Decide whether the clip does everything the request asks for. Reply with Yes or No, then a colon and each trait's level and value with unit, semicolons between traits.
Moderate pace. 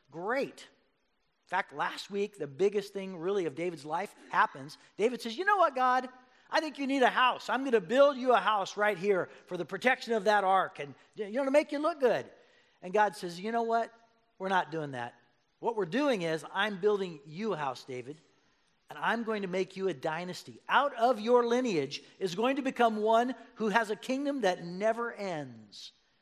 No: fast, 210 wpm